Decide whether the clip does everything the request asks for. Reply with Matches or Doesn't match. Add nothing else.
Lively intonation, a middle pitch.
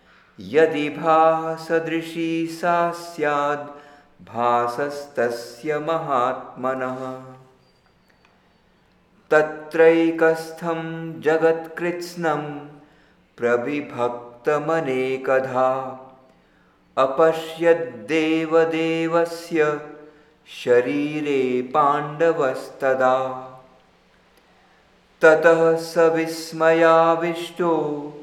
Doesn't match